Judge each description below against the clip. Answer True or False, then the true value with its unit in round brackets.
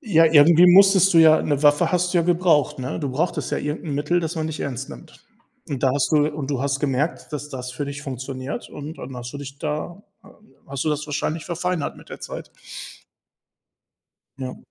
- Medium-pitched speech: True (150 Hz)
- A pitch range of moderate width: True (3.2 semitones)